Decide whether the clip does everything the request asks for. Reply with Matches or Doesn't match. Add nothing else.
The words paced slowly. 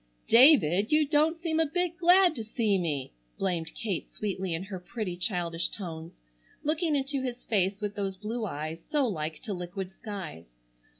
Doesn't match